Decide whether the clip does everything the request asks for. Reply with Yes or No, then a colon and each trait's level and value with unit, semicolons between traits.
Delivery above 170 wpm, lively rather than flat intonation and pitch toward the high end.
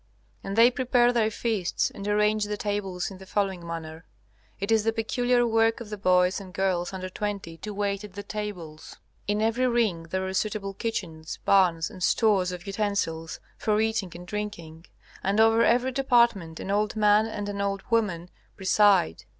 No: average, 180 wpm; average, 3.1 semitones; high, 205 Hz